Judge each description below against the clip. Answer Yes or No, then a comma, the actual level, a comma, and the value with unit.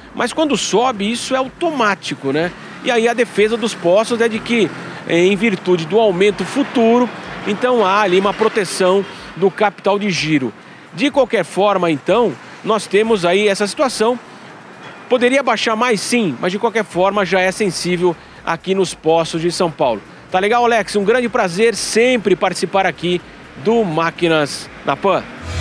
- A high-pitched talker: Yes, high, 200 Hz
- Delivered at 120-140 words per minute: No, average, 160 wpm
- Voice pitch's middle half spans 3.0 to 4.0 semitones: No, average, 4.5 semitones